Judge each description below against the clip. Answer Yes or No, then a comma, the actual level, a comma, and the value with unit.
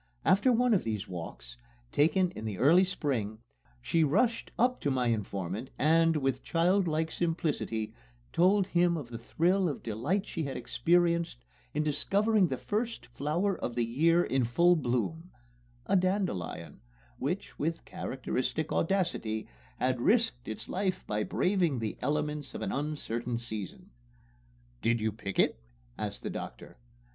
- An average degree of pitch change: No, wide, 7.1 semitones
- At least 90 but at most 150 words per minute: Yes, average, 145 wpm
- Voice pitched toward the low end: No, medium, 150 Hz